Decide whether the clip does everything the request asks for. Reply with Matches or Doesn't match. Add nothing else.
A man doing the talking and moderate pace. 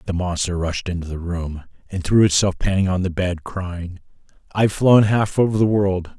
Matches